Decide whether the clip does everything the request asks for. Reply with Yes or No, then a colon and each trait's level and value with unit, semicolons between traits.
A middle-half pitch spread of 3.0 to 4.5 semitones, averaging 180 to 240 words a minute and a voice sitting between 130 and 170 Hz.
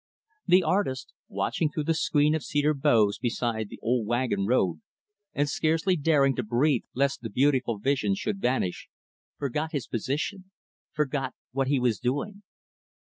No: average, 4.1 semitones; average, 150 wpm; low, 135 Hz